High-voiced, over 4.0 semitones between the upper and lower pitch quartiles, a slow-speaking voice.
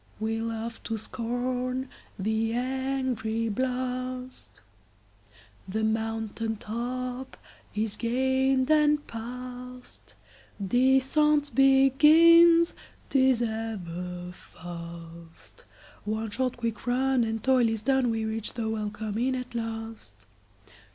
No: high, 230 Hz; average, 3.3 semitones; slow, 90 wpm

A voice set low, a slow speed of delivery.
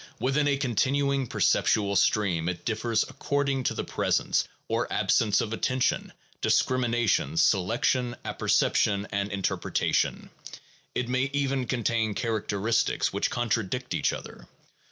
Yes: low, 120 Hz; slow, 115 wpm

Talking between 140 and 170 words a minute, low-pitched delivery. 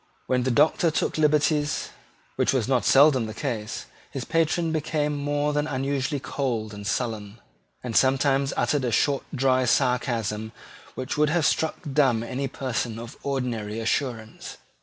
Yes: average, 150 wpm; low, 130 Hz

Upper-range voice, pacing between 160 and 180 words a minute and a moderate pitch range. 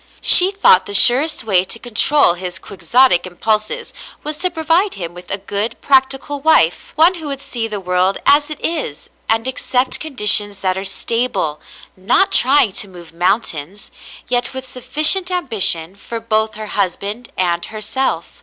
No: high, 225 Hz; average, 165 wpm; wide, 6.5 semitones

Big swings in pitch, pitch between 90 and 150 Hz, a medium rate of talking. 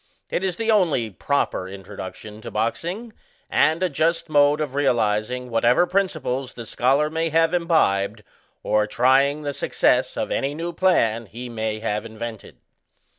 Yes: wide, 6.7 semitones; low, 135 Hz; average, 150 wpm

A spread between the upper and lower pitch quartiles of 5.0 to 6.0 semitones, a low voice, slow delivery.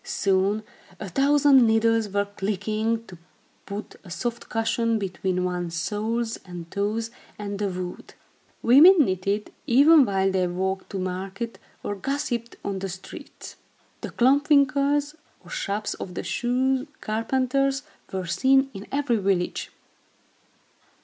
No: wide, 5.4 semitones; high, 215 Hz; slow, 130 wpm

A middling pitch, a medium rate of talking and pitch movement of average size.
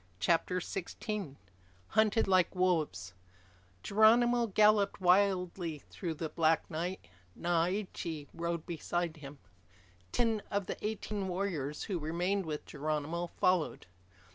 No: medium, 180 Hz; slow, 110 wpm; average, 4.0 semitones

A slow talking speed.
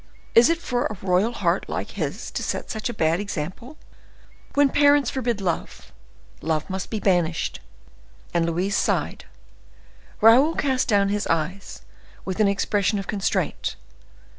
No: average, 145 wpm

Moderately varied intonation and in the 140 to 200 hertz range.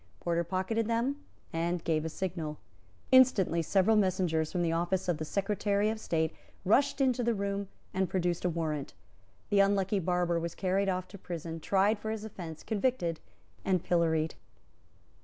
Yes: average, 3.3 semitones; medium, 185 Hz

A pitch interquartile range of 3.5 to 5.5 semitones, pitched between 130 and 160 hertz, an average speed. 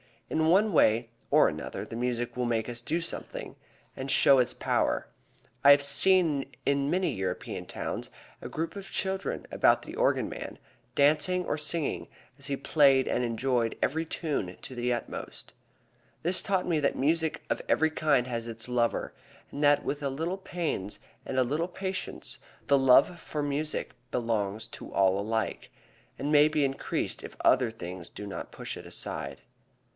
Yes: average, 4.8 semitones; medium, 140 Hz; average, 170 wpm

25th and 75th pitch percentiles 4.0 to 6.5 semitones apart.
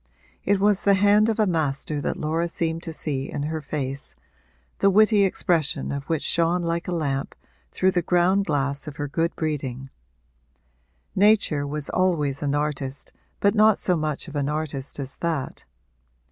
Yes: average, 4.5 semitones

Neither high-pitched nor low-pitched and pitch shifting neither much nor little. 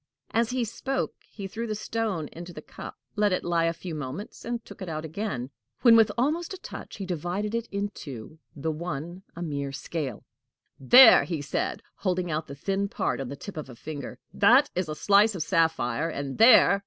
No: medium, 175 Hz; wide, 5.8 semitones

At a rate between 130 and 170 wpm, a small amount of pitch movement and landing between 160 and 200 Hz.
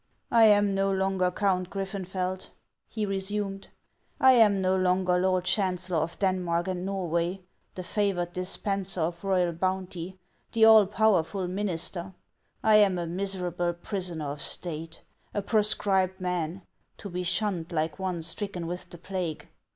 Yes: average, 150 wpm; narrow, 1.9 semitones; medium, 185 Hz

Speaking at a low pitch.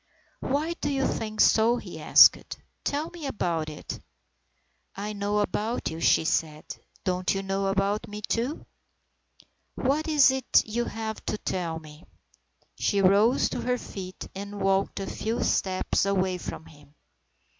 No: high, 200 Hz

